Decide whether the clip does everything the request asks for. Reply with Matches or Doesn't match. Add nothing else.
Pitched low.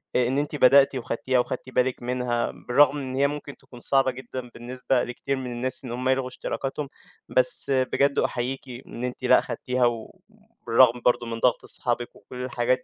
Matches